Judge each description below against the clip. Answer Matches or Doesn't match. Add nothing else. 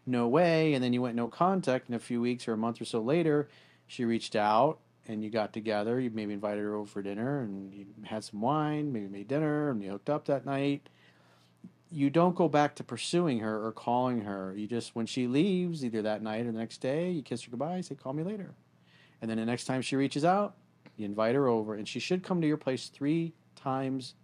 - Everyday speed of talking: Doesn't match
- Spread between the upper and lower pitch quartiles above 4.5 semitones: Matches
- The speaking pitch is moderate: Doesn't match